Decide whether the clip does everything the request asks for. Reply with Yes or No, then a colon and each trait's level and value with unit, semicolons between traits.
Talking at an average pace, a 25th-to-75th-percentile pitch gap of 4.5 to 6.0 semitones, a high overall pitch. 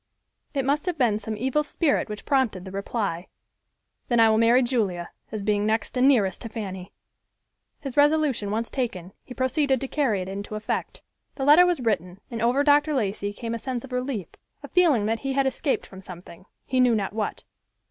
Yes: average, 195 wpm; average, 4.8 semitones; high, 230 Hz